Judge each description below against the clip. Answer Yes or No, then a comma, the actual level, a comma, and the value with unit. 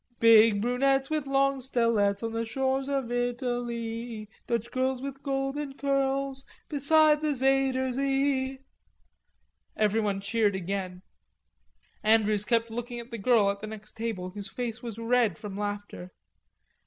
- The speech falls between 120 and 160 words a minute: Yes, slow, 135 wpm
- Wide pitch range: No, average, 3.9 semitones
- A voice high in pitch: Yes, high, 240 Hz